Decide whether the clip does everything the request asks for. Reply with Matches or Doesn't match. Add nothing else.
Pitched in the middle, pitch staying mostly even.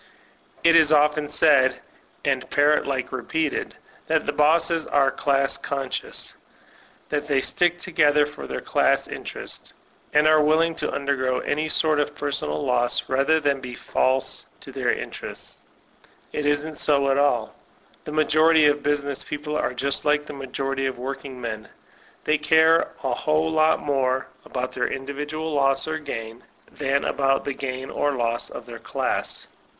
Matches